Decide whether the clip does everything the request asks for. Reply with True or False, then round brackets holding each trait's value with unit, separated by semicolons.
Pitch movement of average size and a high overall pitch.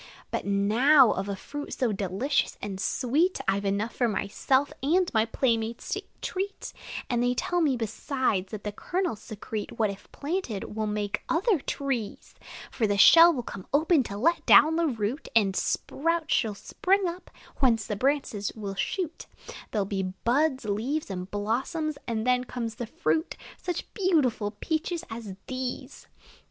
False (6.8 semitones; 240 Hz)